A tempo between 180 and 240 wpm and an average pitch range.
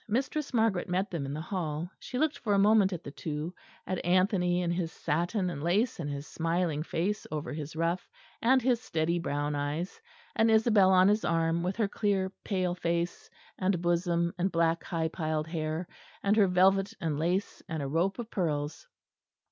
Yes: average, 190 wpm; average, 3.4 semitones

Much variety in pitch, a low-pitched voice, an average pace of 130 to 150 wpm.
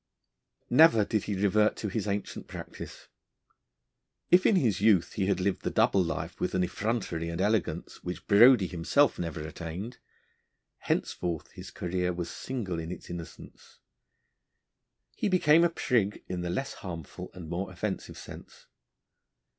No: average, 4.2 semitones; very low, 95 Hz; average, 145 wpm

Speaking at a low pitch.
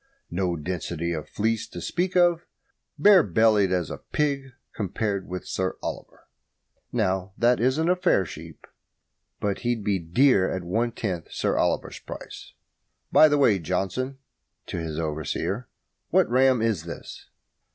Yes: low, 100 Hz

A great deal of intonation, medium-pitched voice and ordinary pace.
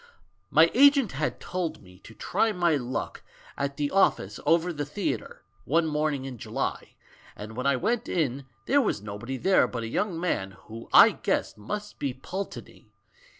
Yes: wide, 6.8 semitones; medium, 145 Hz; average, 170 wpm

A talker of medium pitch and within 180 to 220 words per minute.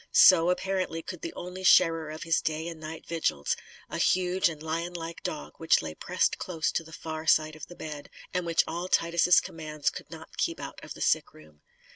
Yes: medium, 165 Hz; fast, 205 wpm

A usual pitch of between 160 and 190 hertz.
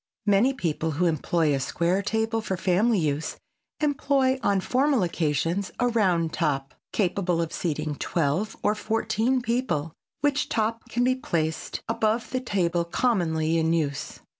Yes: medium, 185 Hz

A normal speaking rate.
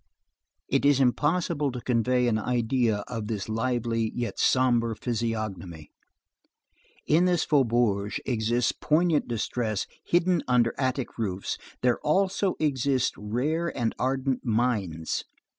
No: slow, 115 wpm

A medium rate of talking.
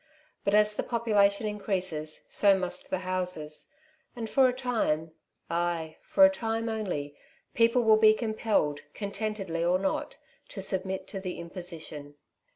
Yes: average, 150 wpm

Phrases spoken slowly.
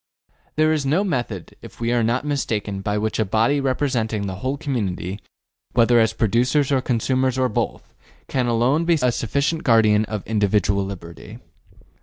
No: average, 165 wpm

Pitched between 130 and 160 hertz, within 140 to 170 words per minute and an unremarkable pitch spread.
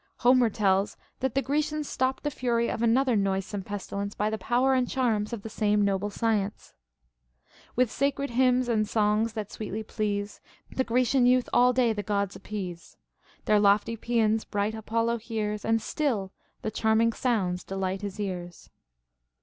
No: high, 220 Hz; average, 165 wpm; average, 3.2 semitones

